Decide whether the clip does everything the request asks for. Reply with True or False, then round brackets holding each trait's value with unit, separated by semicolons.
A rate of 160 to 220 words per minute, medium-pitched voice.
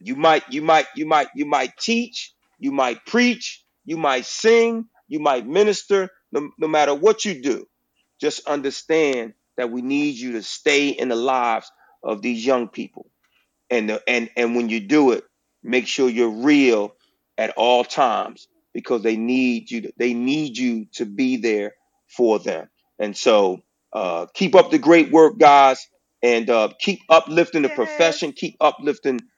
True (170 wpm; 150 Hz)